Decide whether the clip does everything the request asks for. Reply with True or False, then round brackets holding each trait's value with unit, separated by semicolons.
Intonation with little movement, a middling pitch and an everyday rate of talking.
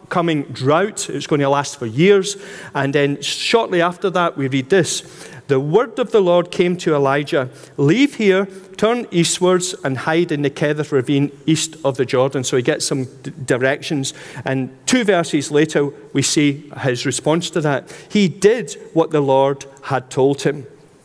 False (4.4 semitones; 150 Hz; 175 wpm)